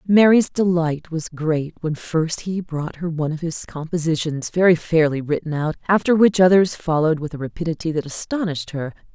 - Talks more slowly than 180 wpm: Yes, average, 170 wpm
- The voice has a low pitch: No, medium, 165 Hz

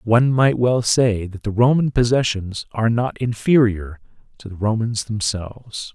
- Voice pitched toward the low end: Yes, low, 115 Hz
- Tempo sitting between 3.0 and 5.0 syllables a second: Yes, 4.6 syllables/s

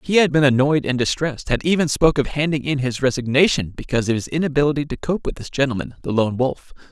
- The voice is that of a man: Yes, male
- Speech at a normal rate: No, fast, 225 wpm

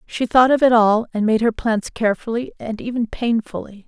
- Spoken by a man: No, female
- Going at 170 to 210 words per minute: Yes, average, 200 wpm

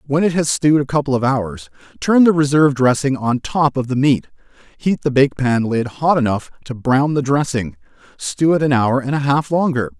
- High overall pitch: No, low, 135 Hz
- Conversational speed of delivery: No, fast, 215 wpm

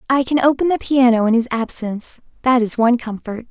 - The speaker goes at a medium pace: Yes, average, 190 wpm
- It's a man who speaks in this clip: No, female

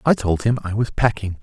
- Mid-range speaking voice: No, low, 110 Hz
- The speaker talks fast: Yes, fast, 255 wpm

